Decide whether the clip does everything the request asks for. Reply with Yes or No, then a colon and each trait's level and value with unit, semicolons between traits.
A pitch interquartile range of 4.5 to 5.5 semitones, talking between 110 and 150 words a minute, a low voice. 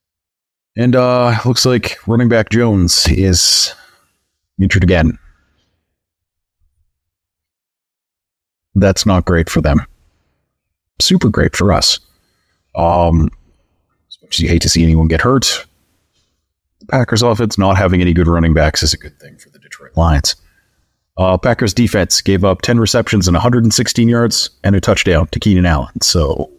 Yes: average, 5.0 semitones; average, 145 wpm; very low, 90 Hz